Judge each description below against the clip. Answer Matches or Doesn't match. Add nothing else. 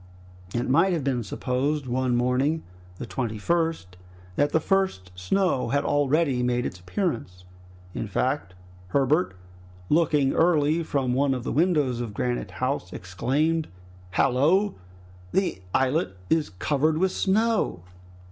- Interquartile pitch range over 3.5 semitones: Matches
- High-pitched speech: Doesn't match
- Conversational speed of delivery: Doesn't match